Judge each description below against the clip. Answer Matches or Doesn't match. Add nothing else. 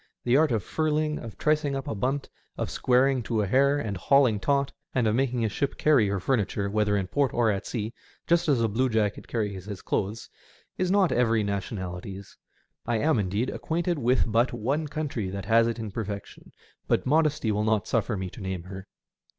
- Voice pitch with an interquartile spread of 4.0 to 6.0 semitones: Matches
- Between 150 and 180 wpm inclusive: Doesn't match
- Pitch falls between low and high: Doesn't match